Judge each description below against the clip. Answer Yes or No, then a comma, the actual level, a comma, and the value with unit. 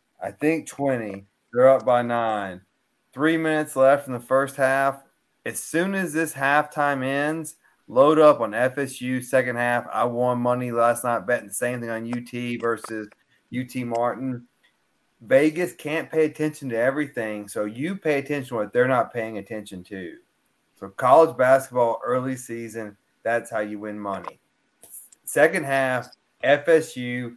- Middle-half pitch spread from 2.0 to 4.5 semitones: Yes, average, 3.6 semitones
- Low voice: Yes, low, 125 Hz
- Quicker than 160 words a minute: No, average, 155 wpm